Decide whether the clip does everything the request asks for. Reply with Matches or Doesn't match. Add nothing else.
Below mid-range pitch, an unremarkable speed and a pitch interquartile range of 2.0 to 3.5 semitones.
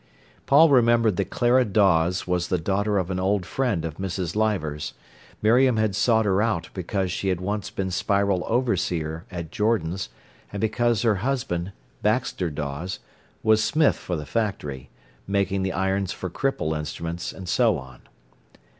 Doesn't match